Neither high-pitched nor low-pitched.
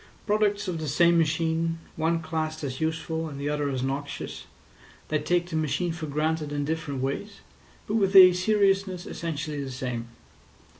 Yes: medium, 160 Hz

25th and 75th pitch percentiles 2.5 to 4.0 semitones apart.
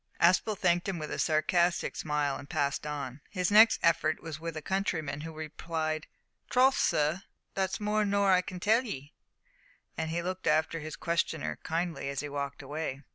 Yes: average, 3.6 semitones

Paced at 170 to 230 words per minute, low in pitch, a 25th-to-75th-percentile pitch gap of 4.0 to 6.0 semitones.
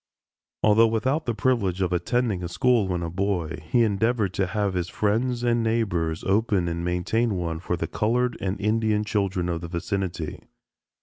Yes: average, 175 wpm; low, 100 Hz; average, 4.4 semitones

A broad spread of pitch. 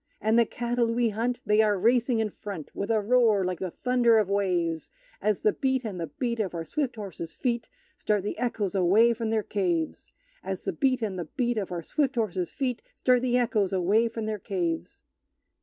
No: average, 4.0 semitones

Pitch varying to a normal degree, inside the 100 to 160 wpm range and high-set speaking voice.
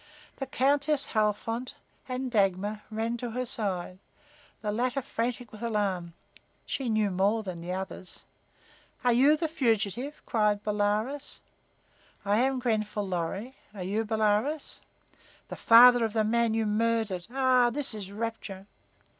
Yes: average, 3.3 semitones; average, 140 wpm; high, 225 Hz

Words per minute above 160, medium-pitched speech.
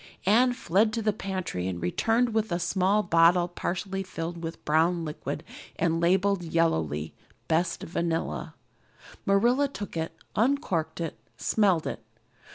No: average, 140 wpm; medium, 175 Hz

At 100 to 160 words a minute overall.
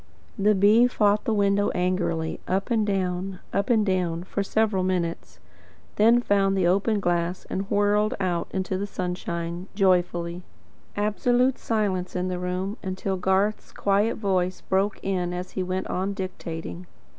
Yes: average, 150 wpm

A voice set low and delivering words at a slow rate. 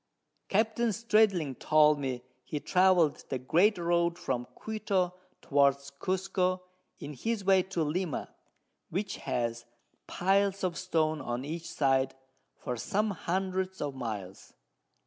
No: medium, 170 Hz; slow, 125 wpm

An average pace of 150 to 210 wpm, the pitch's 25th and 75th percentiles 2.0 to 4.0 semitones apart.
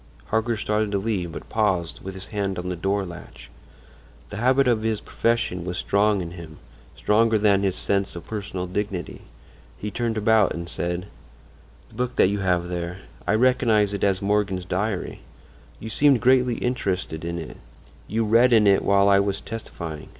Yes: average, 170 wpm; average, 3.6 semitones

